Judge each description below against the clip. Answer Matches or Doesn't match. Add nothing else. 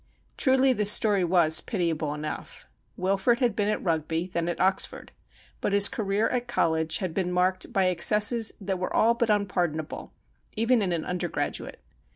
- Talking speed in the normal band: Matches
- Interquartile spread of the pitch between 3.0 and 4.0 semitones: Matches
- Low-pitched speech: Doesn't match